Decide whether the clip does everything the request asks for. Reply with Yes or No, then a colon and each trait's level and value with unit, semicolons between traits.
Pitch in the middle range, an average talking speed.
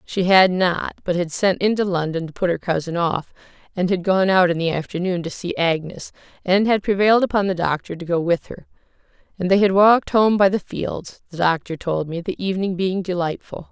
No: medium, 180 Hz; fast, 215 wpm